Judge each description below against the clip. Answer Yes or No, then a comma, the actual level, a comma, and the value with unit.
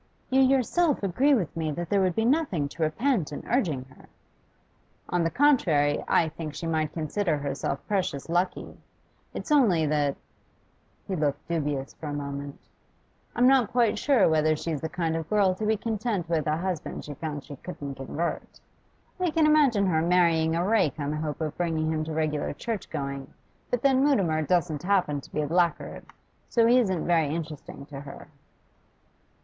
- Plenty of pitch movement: Yes, wide, 5.7 semitones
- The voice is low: No, medium, 165 Hz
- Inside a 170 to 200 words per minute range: Yes, average, 180 wpm